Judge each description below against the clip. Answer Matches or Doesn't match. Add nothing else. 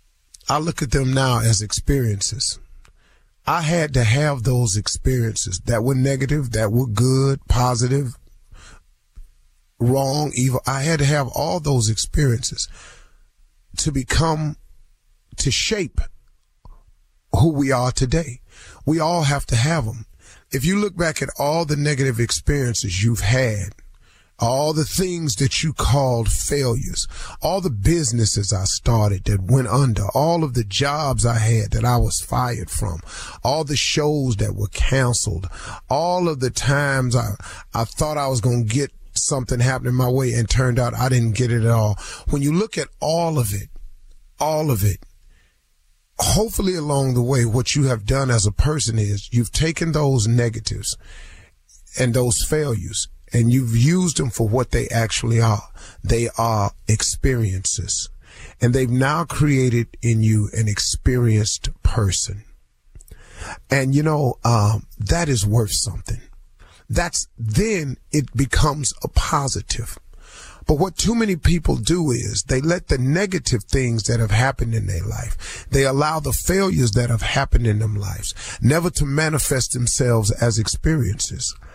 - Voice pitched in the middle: Doesn't match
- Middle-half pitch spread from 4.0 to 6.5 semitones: Matches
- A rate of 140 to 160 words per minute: Matches